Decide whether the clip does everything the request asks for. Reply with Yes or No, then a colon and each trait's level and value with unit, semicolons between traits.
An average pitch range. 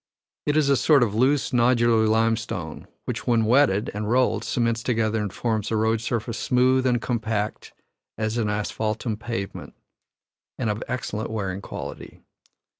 No: narrow, 2.2 semitones